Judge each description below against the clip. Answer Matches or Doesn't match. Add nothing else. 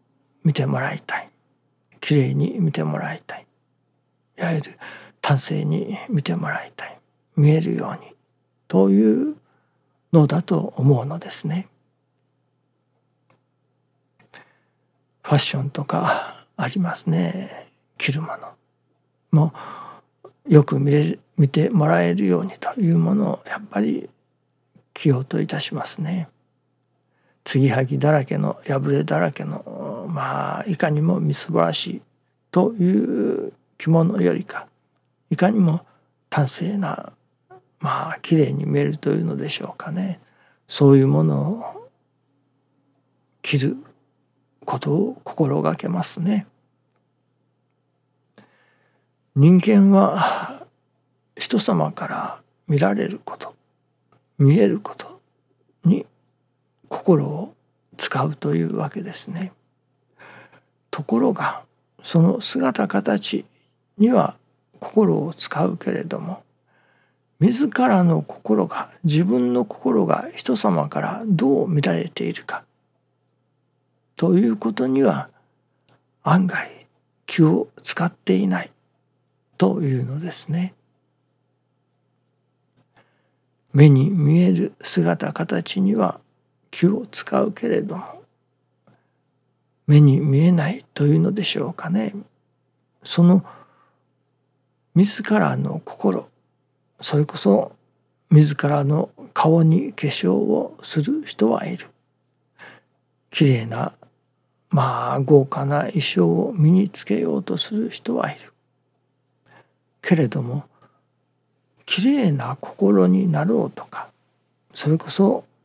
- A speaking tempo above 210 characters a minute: Doesn't match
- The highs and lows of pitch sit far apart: Doesn't match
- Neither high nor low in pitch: Matches